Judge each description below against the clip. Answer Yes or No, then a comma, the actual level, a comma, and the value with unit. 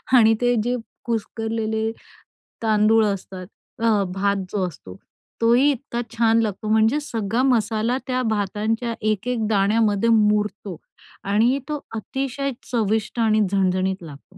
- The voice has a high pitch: Yes, high, 220 Hz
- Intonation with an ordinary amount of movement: No, narrow, 2.2 semitones